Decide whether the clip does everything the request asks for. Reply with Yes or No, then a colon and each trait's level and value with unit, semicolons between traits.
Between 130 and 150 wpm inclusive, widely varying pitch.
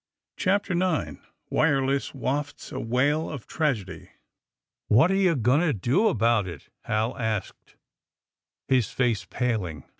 Yes: average, 140 wpm; wide, 5.9 semitones